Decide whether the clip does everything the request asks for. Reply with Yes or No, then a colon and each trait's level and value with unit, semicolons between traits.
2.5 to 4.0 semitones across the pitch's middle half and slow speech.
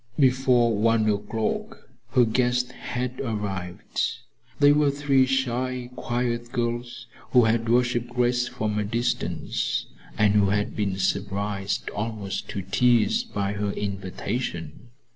Yes: average, 3.3 semitones; slow, 125 wpm